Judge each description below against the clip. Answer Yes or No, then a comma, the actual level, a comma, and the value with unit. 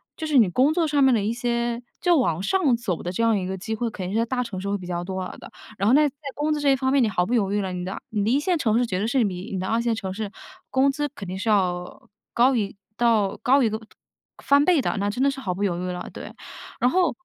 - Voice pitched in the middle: No, high, 225 Hz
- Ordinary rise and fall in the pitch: No, wide, 5.7 semitones